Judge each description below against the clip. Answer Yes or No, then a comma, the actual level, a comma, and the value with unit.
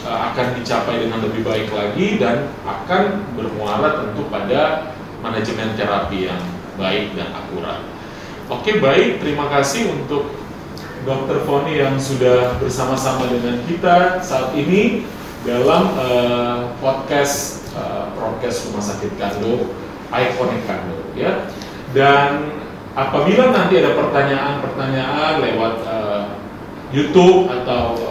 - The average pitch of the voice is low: Yes, low, 130 Hz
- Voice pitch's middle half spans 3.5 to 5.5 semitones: Yes, average, 3.9 semitones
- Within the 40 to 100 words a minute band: No, average, 110 wpm